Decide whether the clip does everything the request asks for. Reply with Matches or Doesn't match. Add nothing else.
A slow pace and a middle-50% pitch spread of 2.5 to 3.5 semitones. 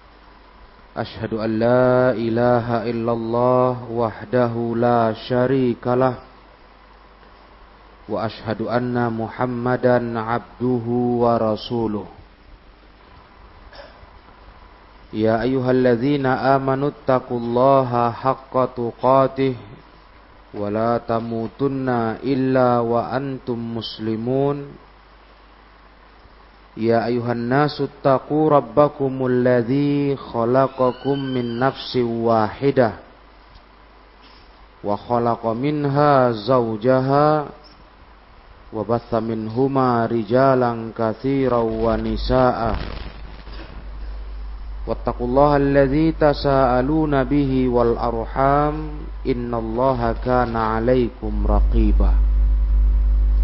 Matches